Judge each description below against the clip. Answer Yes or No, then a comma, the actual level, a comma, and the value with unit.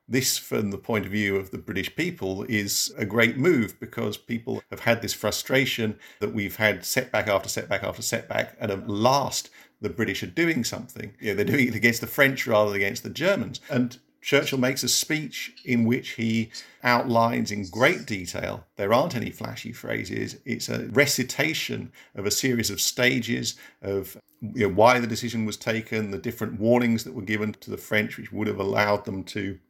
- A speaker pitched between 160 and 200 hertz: No, low, 115 Hz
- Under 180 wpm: No, average, 195 wpm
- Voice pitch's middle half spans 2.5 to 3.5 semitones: Yes, average, 3.2 semitones